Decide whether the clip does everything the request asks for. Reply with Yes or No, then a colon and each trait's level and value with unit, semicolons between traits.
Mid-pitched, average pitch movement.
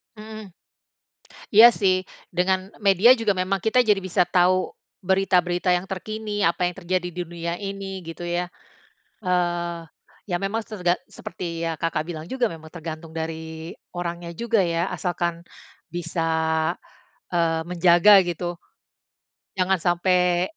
No: medium, 180 Hz; narrow, 2.2 semitones